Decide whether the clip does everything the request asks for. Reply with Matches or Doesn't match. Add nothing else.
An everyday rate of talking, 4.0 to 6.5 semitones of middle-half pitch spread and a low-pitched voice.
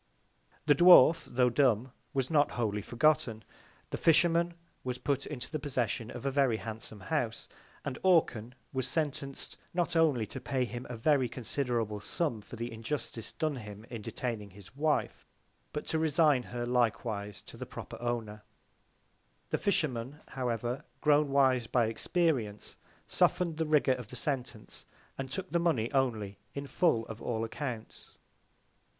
Matches